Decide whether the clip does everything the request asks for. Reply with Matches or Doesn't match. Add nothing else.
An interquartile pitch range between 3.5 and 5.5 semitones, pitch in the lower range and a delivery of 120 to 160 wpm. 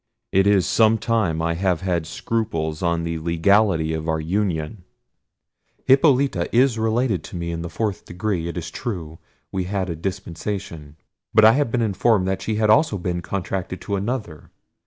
Doesn't match